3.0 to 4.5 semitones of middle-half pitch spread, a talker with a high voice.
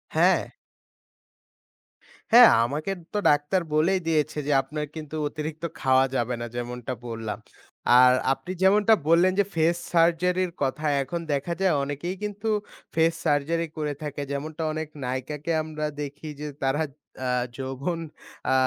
No: average, 3.5 semitones; medium, 155 Hz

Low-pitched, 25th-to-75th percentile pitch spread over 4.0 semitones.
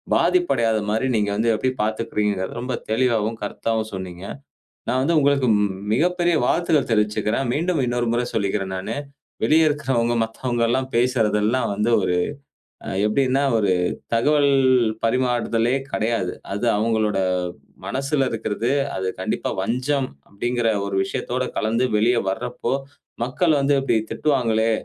No: low, 120 Hz; average, 3.5 semitones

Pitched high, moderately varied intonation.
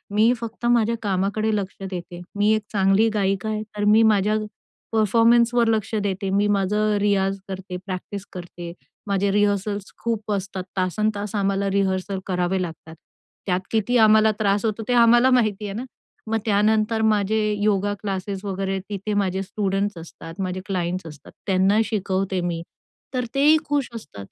No: high, 200 Hz; narrow, 2.2 semitones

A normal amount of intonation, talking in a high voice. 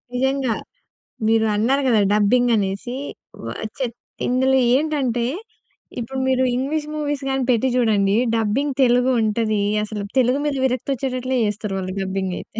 Yes: average, 3.7 semitones; high, 245 Hz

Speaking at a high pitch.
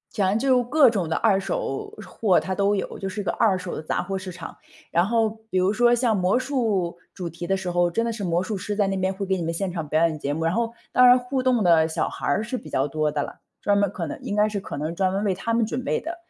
Yes: high, 195 Hz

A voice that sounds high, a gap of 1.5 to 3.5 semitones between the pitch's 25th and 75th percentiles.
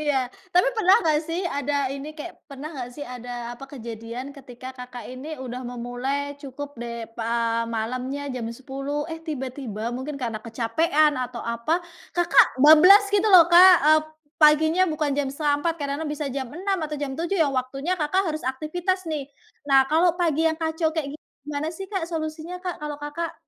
No: very high, 290 Hz; average, 4.0 semitones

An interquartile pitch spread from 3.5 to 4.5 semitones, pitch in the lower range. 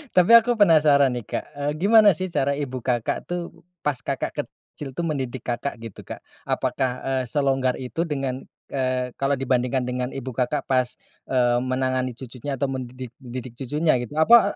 No: average, 2.7 semitones; low, 130 Hz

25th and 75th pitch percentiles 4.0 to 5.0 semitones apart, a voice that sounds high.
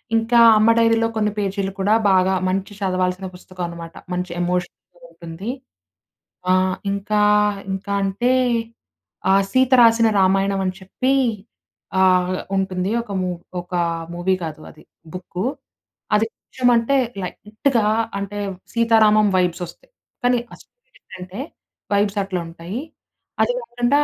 No: average, 3.6 semitones; high, 195 Hz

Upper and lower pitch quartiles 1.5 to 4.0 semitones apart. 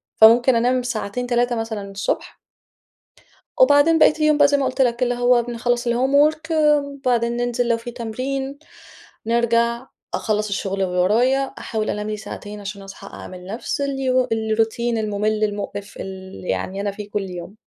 Yes: average, 3.5 semitones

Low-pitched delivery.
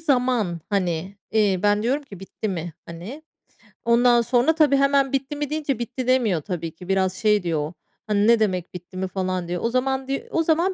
No: high, 215 Hz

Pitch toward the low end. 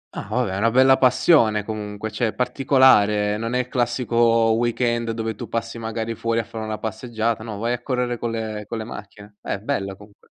Yes: low, 115 Hz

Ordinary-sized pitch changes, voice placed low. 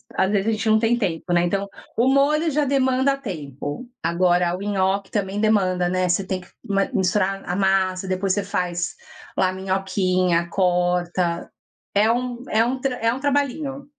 No: average, 4.7 semitones; high, 195 Hz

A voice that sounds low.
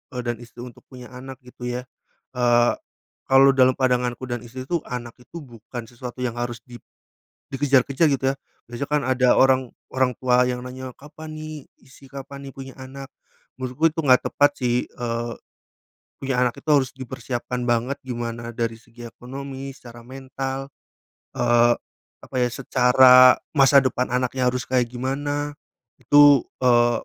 Yes: low, 130 Hz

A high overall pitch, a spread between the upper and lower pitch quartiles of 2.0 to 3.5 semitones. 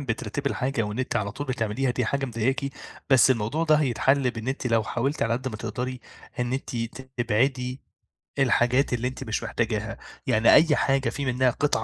No: low, 125 Hz; average, 2.8 semitones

